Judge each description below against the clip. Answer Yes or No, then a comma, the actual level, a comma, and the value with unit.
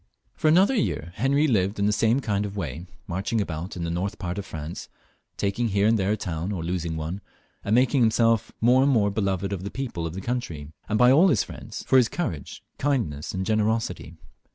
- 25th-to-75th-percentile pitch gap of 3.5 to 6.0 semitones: Yes, average, 5.0 semitones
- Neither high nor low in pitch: No, low, 100 Hz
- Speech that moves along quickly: Yes, fast, 215 wpm